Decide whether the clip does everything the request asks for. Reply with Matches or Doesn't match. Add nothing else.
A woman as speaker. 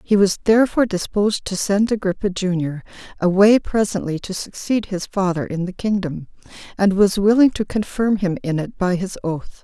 Matches